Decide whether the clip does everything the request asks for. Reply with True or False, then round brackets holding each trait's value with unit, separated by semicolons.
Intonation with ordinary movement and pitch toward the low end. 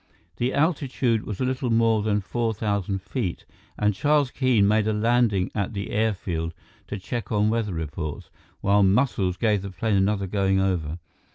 True (3.2 semitones; 105 Hz)